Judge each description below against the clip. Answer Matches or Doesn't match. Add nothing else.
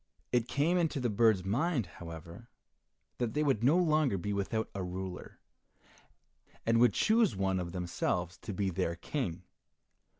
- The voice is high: Doesn't match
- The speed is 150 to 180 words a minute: Matches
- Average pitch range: Doesn't match